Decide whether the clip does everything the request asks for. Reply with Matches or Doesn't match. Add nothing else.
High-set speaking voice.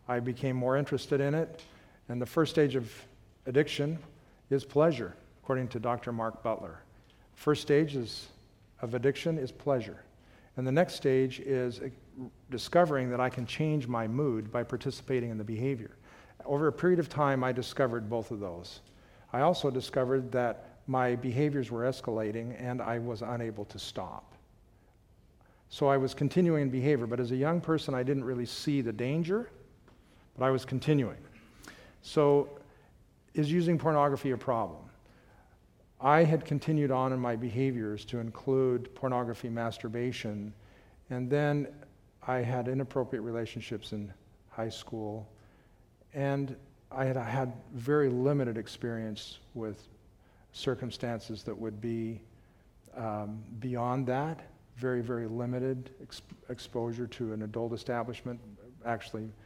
Doesn't match